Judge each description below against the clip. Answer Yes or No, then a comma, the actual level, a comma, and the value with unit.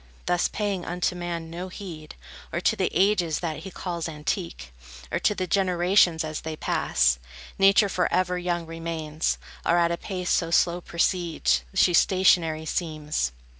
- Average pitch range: No, narrow, 2.3 semitones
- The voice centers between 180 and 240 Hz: No, medium, 170 Hz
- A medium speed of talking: Yes, average, 155 wpm